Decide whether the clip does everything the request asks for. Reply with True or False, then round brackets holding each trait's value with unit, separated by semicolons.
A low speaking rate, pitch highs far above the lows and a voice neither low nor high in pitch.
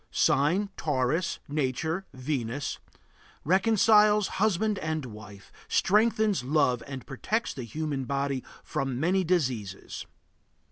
True (100 wpm; 6.7 semitones; 150 Hz)